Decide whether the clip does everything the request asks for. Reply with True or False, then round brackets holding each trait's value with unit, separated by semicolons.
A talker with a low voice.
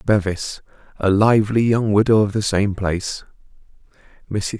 True (105 Hz)